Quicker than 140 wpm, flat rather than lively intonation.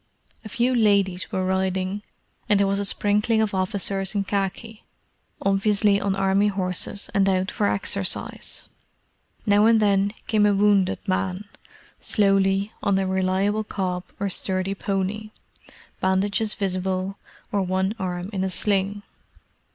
No: slow, 135 wpm; narrow, 1.5 semitones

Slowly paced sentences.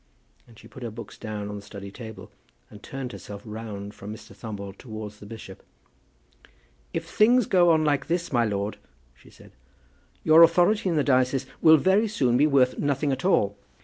No: average, 185 wpm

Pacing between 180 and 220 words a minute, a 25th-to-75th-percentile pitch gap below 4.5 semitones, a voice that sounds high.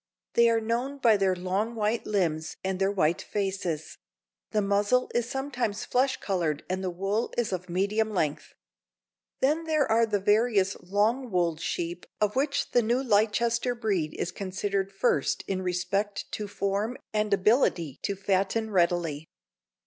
No: average, 155 wpm; average, 3.8 semitones; high, 205 Hz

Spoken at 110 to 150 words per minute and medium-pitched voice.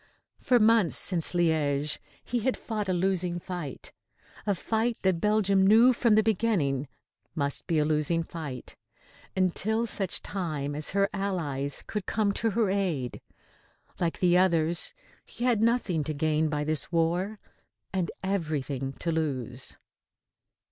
Yes: average, 140 wpm; medium, 175 Hz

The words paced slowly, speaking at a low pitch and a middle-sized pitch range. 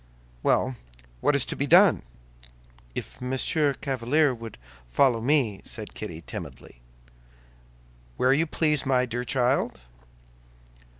Yes: slow, 115 wpm; low, 130 Hz; average, 3.2 semitones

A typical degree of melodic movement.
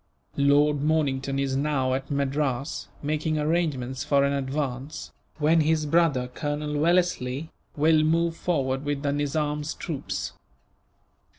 No: narrow, 2.2 semitones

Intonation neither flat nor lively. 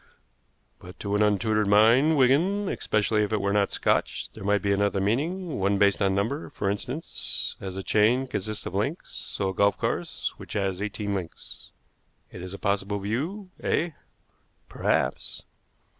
Yes: average, 4.2 semitones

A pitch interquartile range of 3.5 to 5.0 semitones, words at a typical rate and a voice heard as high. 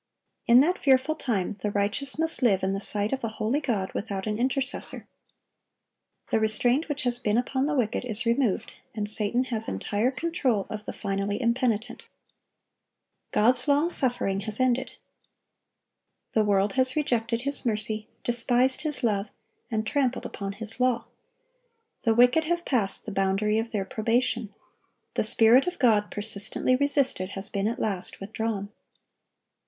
Yes: average, 3.8 semitones; average, 155 wpm; high, 230 Hz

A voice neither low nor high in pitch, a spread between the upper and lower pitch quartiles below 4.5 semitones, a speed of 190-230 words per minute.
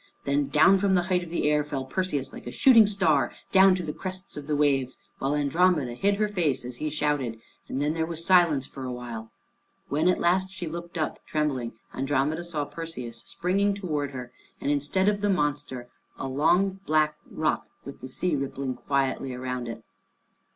No: medium, 150 Hz; average, 5.0 semitones; average, 195 wpm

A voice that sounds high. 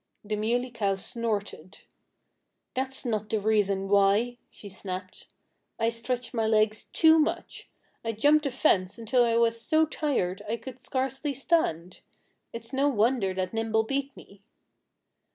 Yes: high, 230 Hz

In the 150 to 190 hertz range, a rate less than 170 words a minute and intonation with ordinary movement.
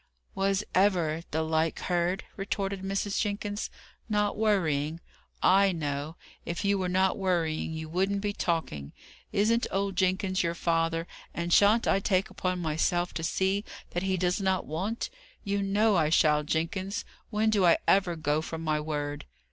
Yes: medium, 185 Hz; average, 160 wpm; average, 3.5 semitones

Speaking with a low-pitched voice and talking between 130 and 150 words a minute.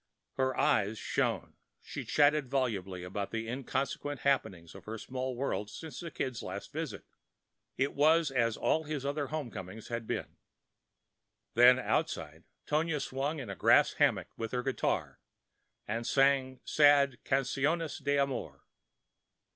Yes: low, 130 Hz; average, 140 wpm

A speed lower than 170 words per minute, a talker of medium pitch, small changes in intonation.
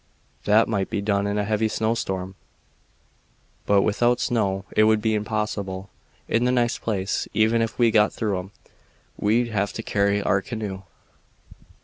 No: average, 155 wpm; low, 105 Hz; narrow, 2.1 semitones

